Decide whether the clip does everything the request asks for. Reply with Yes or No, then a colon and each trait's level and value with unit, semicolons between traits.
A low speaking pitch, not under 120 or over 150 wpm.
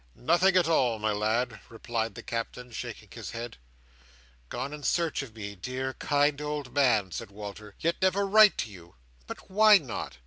No: low, 125 Hz; average, 175 wpm